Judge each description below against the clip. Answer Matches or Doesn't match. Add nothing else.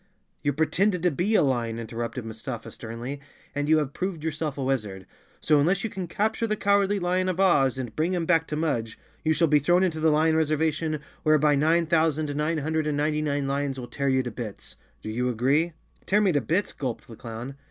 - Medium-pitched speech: Matches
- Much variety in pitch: Doesn't match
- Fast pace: Matches